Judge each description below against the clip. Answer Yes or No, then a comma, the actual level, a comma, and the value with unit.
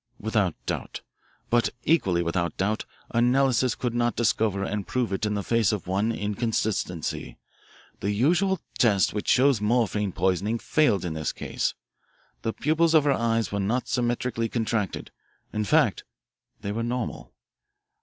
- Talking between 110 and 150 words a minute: Yes, average, 145 wpm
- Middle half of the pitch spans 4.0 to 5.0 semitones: No, average, 3.3 semitones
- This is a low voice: Yes, low, 110 Hz